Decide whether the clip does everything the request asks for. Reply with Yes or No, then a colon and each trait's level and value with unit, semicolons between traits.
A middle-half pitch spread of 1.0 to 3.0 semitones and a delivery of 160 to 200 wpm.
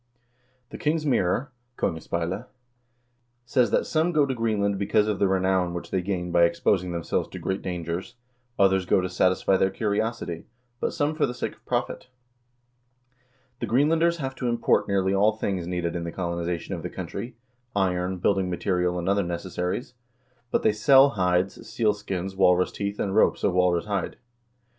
No: average, 3.8 semitones; average, 170 wpm